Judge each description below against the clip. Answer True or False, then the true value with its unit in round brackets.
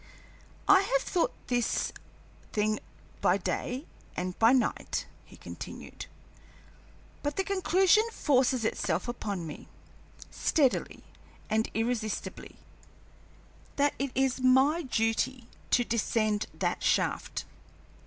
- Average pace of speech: False (105 wpm)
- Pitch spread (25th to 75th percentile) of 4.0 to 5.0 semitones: True (4.7 semitones)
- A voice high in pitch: True (250 Hz)